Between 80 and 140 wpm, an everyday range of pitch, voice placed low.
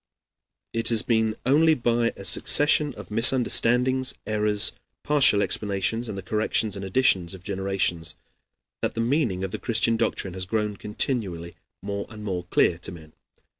No: average, 155 wpm; average, 3.6 semitones; low, 105 Hz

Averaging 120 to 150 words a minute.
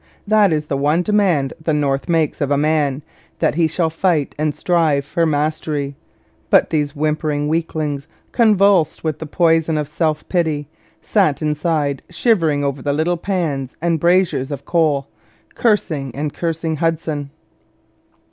Yes: average, 145 wpm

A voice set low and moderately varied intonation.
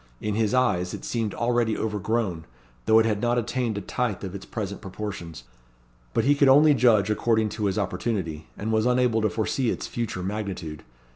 Yes: low, 110 Hz; average, 3.2 semitones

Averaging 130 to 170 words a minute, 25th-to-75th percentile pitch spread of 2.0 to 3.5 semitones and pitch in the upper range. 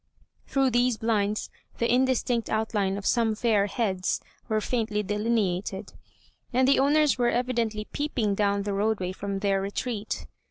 Yes: average, 145 wpm; average, 3.2 semitones; high, 220 Hz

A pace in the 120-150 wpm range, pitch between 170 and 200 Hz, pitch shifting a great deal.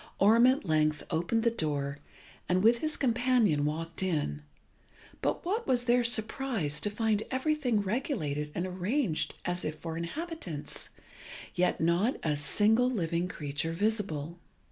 Yes: average, 140 wpm; high, 190 Hz; wide, 7.2 semitones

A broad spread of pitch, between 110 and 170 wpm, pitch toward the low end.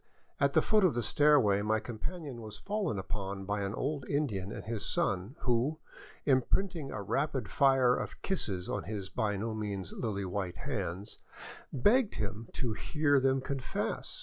Yes: wide, 5.8 semitones; average, 165 wpm; low, 115 Hz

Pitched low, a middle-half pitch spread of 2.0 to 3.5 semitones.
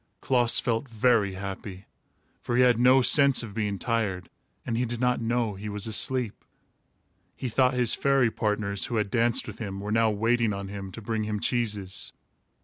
Yes: low, 115 Hz; average, 3.1 semitones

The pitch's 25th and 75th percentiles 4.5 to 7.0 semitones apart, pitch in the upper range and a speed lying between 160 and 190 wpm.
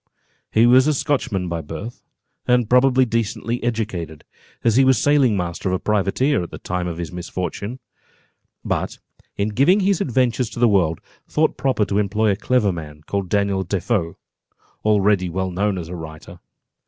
No: wide, 5.4 semitones; low, 105 Hz; average, 170 wpm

